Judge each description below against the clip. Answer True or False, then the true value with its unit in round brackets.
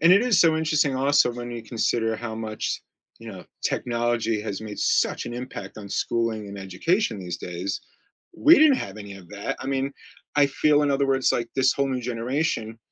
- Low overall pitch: True (120 Hz)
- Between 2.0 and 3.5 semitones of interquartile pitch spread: False (4.4 semitones)